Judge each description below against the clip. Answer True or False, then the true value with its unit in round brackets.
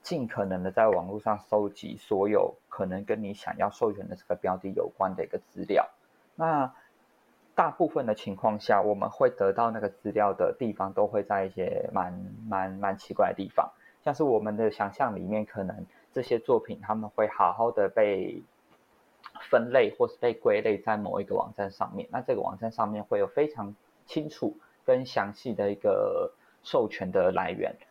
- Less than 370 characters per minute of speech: True (270 characters per minute)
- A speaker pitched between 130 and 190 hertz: False (325 Hz)